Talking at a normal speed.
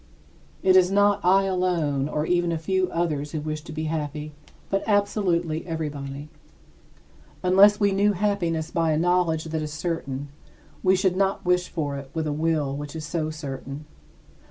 Yes: average, 170 wpm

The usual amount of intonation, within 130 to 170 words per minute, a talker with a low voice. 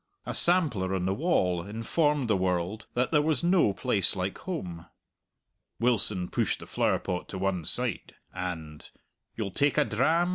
No: wide, 8.3 semitones; average, 155 wpm; low, 105 Hz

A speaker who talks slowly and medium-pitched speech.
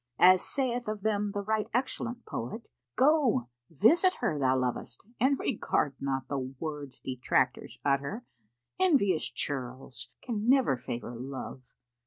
Yes: slow, 130 wpm; medium, 170 Hz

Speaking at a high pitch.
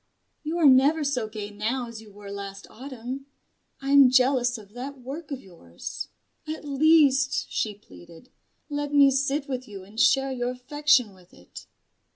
Yes: very high, 255 Hz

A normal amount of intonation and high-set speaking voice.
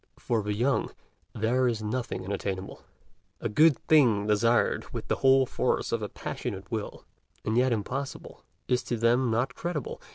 No: average, 3.5 semitones; low, 115 Hz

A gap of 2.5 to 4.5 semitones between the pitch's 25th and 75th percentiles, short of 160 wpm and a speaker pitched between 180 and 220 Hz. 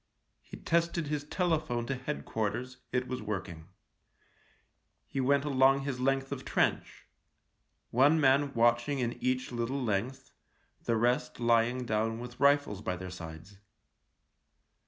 No: average, 3.2 semitones; average, 140 wpm; low, 125 Hz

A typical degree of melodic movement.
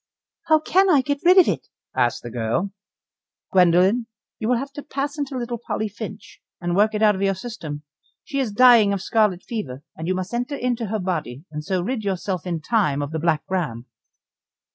No: wide, 5.9 semitones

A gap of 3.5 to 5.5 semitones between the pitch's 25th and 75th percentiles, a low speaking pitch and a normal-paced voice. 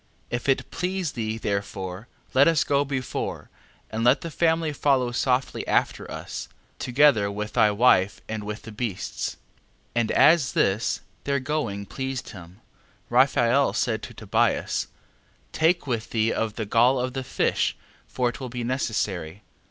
Yes: average, 4.3 semitones; low, 120 Hz; average, 160 wpm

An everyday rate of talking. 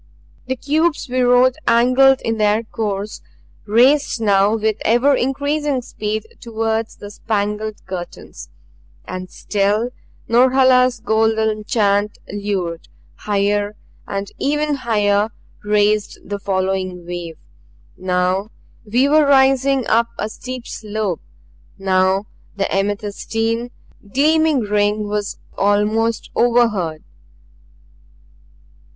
No: slow, 100 wpm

